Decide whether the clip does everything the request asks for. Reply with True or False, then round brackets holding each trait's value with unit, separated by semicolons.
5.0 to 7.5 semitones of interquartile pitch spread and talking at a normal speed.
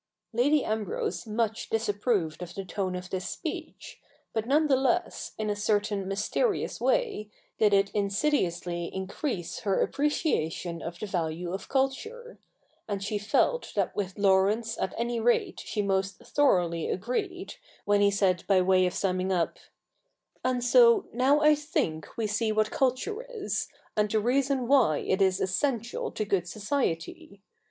True (5.6 semitones; 155 wpm)